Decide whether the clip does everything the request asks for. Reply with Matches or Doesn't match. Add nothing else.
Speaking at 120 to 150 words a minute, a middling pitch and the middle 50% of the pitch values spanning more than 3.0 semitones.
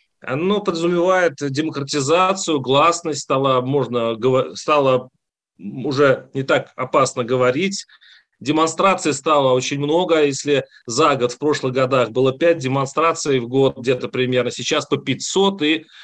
Matches